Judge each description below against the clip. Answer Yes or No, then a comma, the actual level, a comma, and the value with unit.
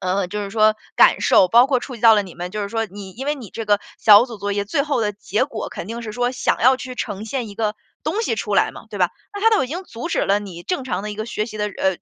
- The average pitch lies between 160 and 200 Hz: No, high, 215 Hz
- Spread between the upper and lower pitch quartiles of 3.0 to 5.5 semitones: Yes, average, 3.8 semitones